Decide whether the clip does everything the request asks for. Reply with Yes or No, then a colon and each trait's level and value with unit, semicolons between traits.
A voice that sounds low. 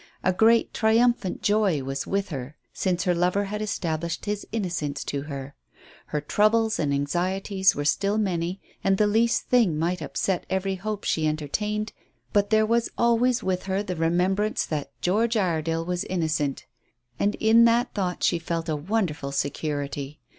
No: medium, 185 Hz